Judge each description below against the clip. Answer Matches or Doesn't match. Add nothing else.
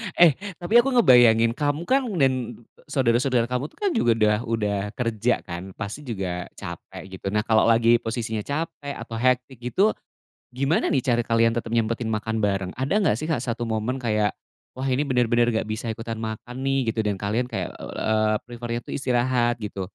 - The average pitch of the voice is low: Matches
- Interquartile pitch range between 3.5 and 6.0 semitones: Doesn't match